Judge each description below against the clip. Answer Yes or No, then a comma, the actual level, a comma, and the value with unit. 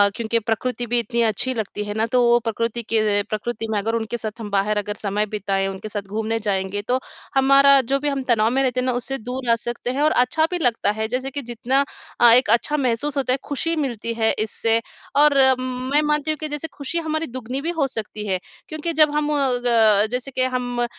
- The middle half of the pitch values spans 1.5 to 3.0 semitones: No, average, 3.7 semitones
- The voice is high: Yes, high, 240 Hz